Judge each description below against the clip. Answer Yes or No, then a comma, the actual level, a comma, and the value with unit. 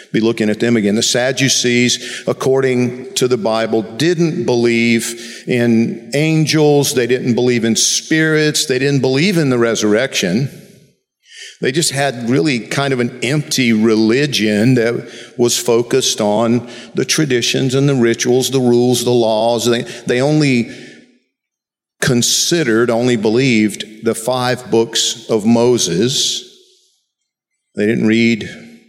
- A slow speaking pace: Yes, slow, 130 wpm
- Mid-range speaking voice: No, low, 120 Hz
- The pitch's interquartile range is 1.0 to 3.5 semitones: Yes, average, 2.8 semitones